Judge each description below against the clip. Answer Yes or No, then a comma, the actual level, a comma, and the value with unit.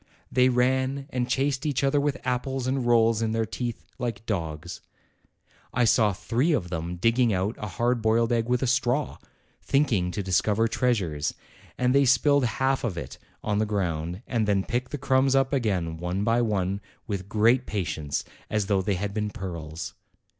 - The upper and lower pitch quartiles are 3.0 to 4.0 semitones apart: No, average, 4.8 semitones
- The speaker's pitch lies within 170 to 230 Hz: No, low, 115 Hz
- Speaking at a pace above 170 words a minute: Yes, average, 180 wpm